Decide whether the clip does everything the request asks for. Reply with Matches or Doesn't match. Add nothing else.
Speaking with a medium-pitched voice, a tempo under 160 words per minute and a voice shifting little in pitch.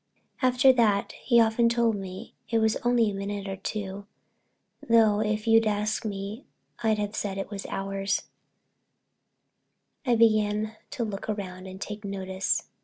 Doesn't match